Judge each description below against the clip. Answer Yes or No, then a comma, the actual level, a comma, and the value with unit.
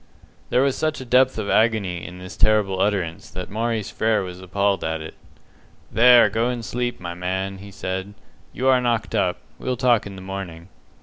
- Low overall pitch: Yes, low, 100 Hz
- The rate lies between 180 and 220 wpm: Yes, average, 190 wpm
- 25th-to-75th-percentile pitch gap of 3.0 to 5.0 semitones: Yes, average, 4.2 semitones